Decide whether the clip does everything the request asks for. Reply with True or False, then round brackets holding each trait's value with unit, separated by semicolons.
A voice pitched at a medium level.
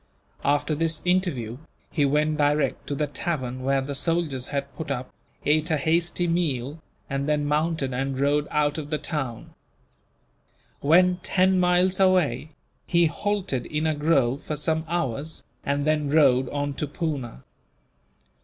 True (150 Hz)